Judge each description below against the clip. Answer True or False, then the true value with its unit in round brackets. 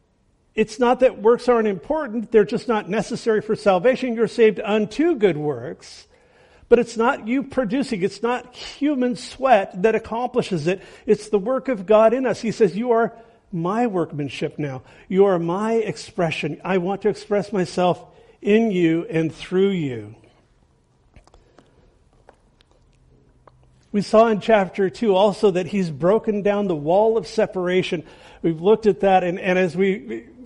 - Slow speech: False (155 wpm)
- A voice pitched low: False (205 Hz)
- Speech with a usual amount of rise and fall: True (4.1 semitones)